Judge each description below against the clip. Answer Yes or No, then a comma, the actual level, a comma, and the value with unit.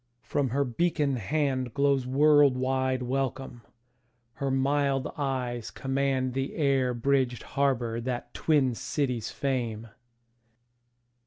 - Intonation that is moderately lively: No, narrow, 1.9 semitones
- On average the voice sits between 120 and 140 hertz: Yes, low, 135 Hz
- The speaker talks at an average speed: No, slow, 95 wpm